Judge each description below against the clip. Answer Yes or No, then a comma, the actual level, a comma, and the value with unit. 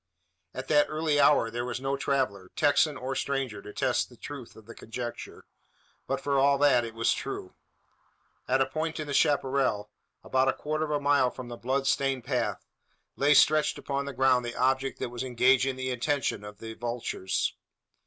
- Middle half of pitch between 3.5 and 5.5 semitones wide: No, average, 2.7 semitones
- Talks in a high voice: No, low, 130 Hz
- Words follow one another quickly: No, average, 190 wpm